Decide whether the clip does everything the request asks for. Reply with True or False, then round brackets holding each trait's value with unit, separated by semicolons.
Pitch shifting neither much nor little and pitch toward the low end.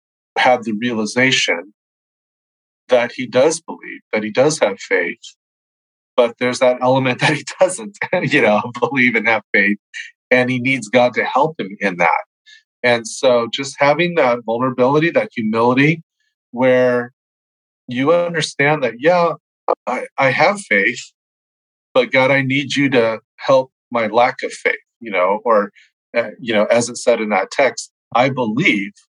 True (4.6 semitones; 130 Hz)